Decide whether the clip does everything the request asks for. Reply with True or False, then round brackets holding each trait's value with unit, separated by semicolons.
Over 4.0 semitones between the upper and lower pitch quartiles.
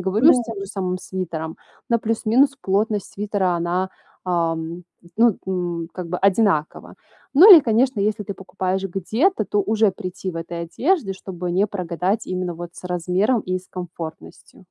False (3.3 semitones)